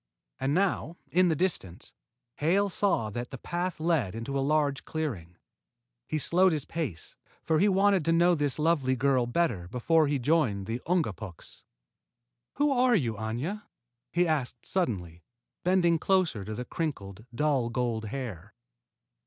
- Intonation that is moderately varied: No, wide, 6.7 semitones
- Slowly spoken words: No, average, 150 wpm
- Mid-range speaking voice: Yes, medium, 145 Hz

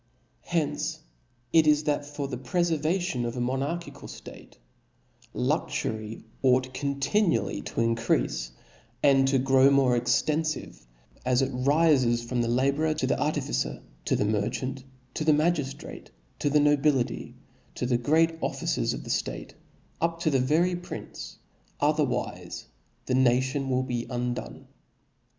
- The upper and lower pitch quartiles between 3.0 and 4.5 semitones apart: Yes, average, 3.7 semitones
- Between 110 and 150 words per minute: Yes, slow, 135 wpm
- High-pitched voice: No, low, 135 Hz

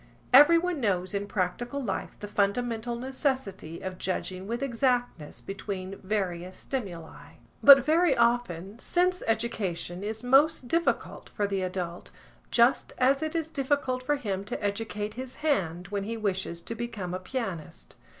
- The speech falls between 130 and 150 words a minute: Yes, average, 145 wpm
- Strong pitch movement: Yes, wide, 5.7 semitones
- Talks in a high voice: Yes, high, 220 Hz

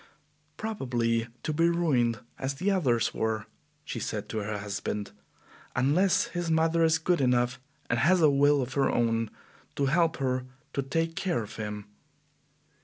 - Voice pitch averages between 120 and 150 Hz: Yes, low, 135 Hz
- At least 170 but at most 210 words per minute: No, average, 160 wpm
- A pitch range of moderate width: No, wide, 5.9 semitones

